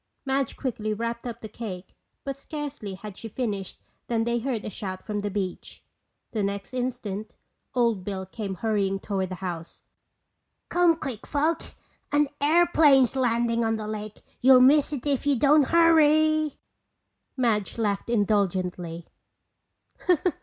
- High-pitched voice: Yes, high, 230 Hz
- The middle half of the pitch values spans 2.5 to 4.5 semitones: No, average, 5.3 semitones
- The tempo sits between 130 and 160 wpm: Yes, average, 140 wpm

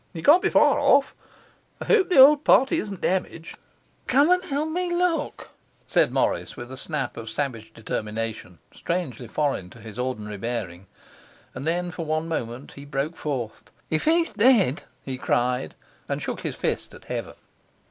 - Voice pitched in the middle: Yes, medium, 155 Hz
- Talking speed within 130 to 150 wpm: No, average, 170 wpm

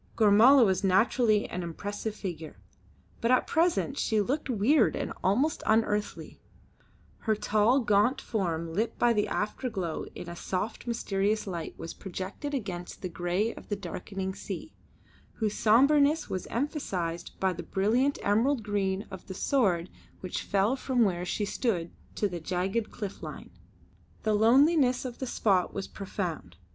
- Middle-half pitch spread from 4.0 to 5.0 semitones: Yes, average, 4.3 semitones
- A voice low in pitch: No, high, 210 Hz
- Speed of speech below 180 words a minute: Yes, average, 150 wpm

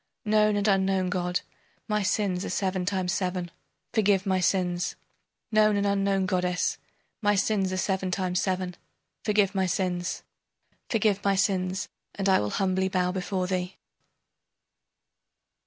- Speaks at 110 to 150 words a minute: Yes, average, 140 wpm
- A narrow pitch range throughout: Yes, narrow, 1.7 semitones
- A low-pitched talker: No, high, 190 Hz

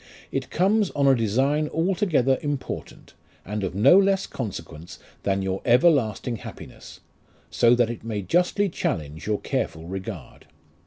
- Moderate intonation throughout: No, wide, 7.8 semitones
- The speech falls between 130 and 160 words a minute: Yes, average, 140 wpm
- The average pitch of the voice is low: Yes, low, 120 Hz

